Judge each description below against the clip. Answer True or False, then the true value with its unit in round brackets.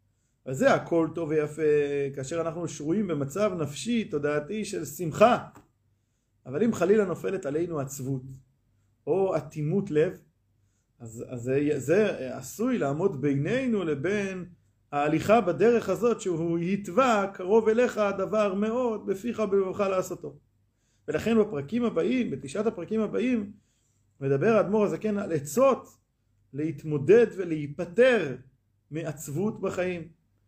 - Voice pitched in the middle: True (160 Hz)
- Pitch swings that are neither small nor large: False (7.1 semitones)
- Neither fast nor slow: True (110 wpm)